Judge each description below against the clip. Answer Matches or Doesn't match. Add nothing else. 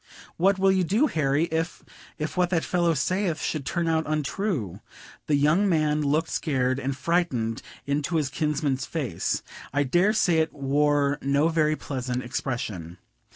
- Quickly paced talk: Doesn't match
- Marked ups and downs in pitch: Doesn't match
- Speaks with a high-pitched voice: Doesn't match